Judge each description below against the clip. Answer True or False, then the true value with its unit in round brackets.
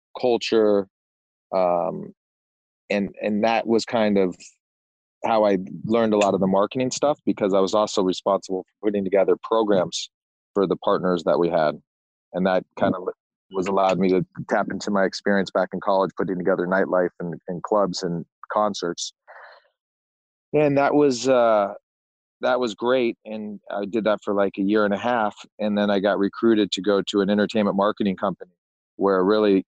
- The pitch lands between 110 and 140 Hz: False (100 Hz)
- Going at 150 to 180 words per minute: True (175 wpm)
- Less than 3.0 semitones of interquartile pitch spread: True (2.6 semitones)